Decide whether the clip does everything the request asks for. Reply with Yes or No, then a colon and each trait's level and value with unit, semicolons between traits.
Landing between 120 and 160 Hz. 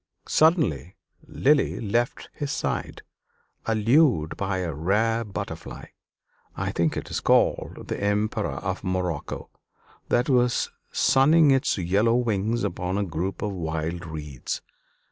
No: low, 100 Hz